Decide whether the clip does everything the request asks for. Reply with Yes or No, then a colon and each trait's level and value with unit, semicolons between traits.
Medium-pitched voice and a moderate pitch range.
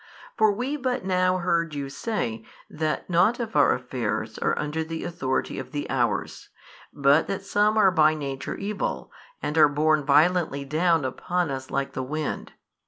Yes: medium, 160 Hz; average, 4.7 semitones